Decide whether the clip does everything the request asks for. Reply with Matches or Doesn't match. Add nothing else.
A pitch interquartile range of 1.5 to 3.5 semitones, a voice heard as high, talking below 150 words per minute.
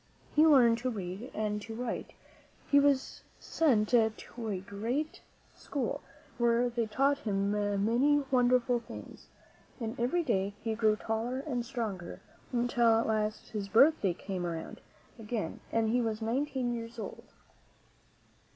Matches